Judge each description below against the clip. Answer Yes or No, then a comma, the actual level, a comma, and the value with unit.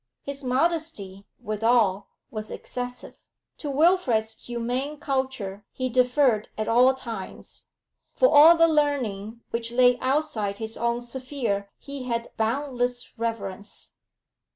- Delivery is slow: Yes, slow, 115 wpm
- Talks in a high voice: Yes, high, 245 Hz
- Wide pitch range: No, average, 3.8 semitones